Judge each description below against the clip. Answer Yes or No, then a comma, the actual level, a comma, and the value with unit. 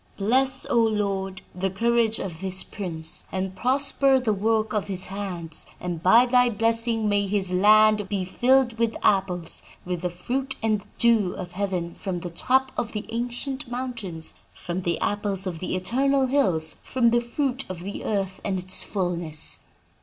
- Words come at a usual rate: Yes, average, 170 wpm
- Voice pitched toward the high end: Yes, high, 205 Hz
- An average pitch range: Yes, average, 4.4 semitones